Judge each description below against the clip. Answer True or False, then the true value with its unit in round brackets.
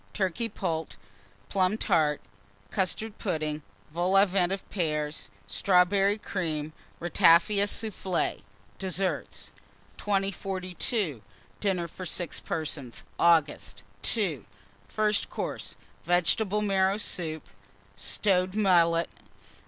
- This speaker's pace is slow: True (90 wpm)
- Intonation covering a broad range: False (3.2 semitones)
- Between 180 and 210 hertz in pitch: True (185 Hz)